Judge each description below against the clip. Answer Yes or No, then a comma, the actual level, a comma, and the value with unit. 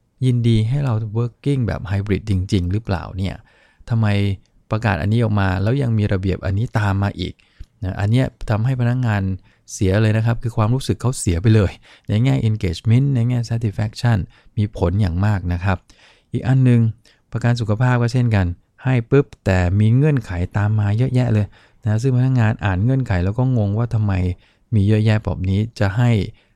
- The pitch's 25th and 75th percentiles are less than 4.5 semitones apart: Yes, average, 3.3 semitones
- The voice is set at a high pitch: No, low, 110 Hz